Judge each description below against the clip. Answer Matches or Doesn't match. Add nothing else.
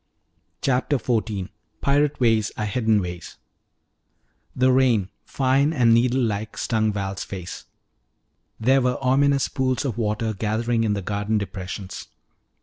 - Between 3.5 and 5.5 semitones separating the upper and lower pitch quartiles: Matches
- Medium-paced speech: Doesn't match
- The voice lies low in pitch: Matches